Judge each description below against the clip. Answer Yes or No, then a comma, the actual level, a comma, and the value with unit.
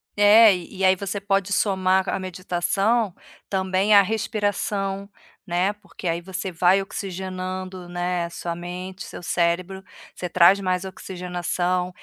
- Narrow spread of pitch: Yes, narrow, 1.7 semitones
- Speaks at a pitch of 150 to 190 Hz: Yes, medium, 185 Hz